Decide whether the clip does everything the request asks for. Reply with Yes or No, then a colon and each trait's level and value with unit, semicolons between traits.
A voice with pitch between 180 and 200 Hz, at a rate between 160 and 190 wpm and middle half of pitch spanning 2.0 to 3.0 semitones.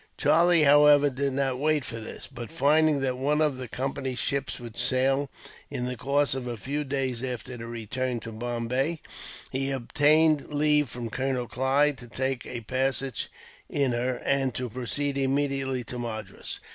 No: low, 130 Hz; average, 170 wpm; narrow, 2.5 semitones